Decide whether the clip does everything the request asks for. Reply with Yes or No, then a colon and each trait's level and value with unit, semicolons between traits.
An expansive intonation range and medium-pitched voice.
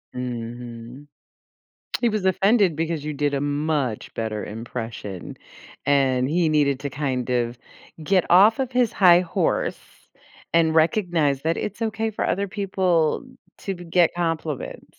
Yes: wide, 6.1 semitones; medium, 155 Hz